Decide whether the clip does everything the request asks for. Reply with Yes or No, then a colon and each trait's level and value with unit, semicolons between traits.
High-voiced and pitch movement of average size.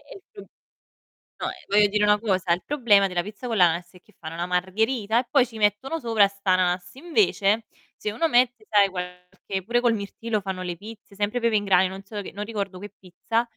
Yes: high, 205 Hz; average, 3.6 semitones